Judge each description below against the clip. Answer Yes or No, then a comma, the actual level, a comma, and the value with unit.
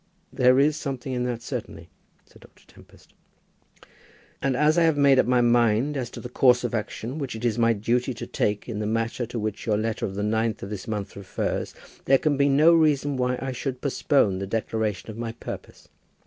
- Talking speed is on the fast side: Yes, fast, 215 wpm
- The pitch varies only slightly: No, average, 3.7 semitones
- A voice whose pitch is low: Yes, low, 120 Hz